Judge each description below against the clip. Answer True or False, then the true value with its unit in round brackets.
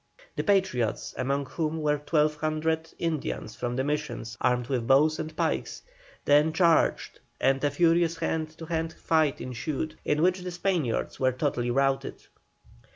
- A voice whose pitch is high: False (150 Hz)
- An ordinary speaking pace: True (150 wpm)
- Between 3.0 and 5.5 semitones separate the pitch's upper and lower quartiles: True (3.3 semitones)